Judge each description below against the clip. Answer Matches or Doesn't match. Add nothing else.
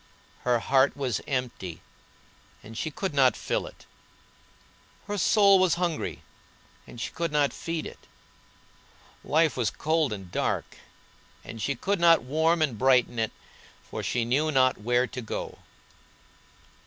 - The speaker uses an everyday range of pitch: Matches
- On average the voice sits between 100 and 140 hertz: Matches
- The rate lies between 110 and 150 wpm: Matches